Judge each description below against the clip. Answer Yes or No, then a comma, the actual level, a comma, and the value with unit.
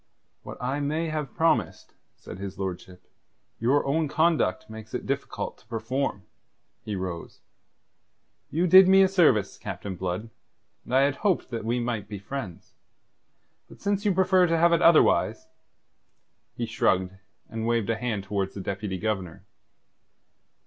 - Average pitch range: No, wide, 8.3 semitones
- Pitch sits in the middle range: No, low, 115 Hz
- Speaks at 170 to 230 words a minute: No, average, 150 wpm